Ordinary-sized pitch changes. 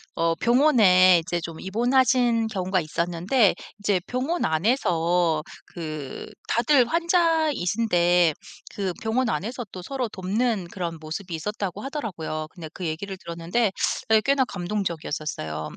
No: wide, 6.0 semitones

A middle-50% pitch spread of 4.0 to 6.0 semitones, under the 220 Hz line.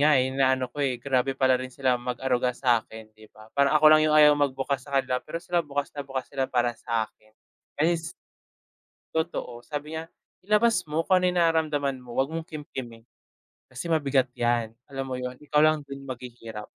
No: average, 3.4 semitones; low, 135 Hz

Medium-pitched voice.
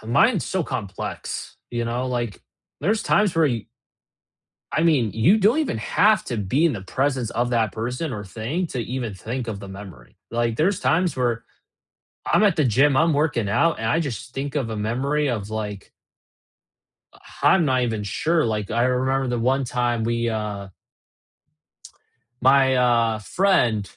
No: low, 120 Hz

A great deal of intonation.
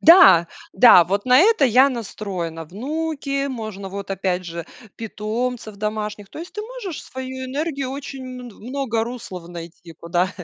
Yes: wide, 6.2 semitones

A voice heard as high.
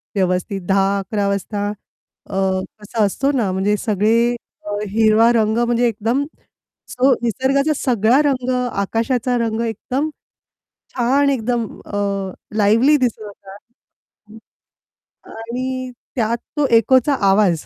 Yes: high, 225 Hz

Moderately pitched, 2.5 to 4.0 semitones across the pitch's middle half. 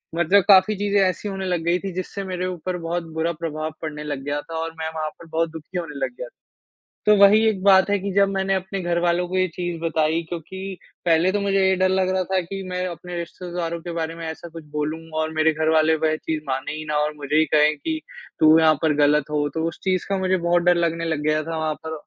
Yes: medium, 170 Hz; average, 2.9 semitones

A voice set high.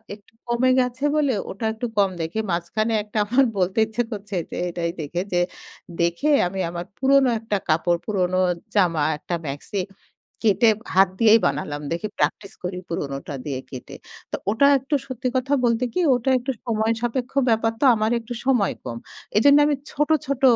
Yes: high, 215 Hz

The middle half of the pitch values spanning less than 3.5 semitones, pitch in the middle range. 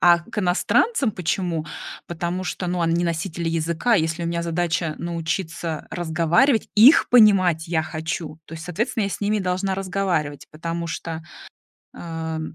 Yes: narrow, 2.6 semitones; medium, 170 Hz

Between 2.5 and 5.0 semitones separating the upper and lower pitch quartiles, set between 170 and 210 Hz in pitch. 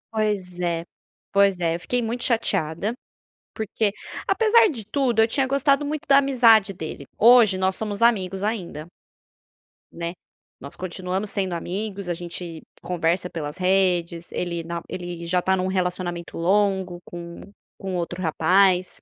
Yes: average, 3.9 semitones; medium, 185 Hz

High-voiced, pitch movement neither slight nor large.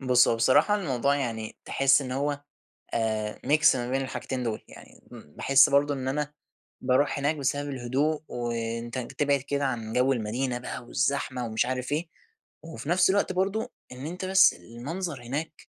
No: low, 135 Hz; average, 3.2 semitones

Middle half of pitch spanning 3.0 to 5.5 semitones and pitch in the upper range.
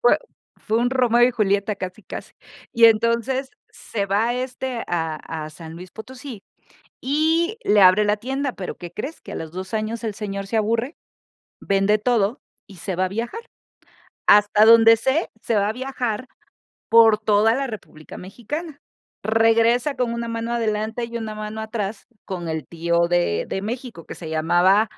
Yes: average, 3.5 semitones; high, 220 Hz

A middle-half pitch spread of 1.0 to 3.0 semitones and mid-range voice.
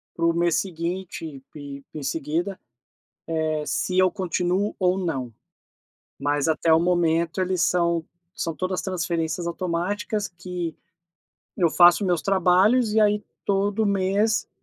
Yes: narrow, 2.5 semitones; medium, 180 Hz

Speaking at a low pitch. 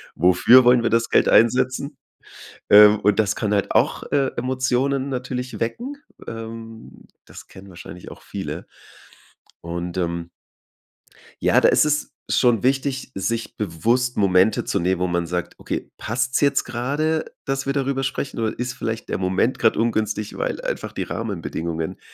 Yes: low, 115 Hz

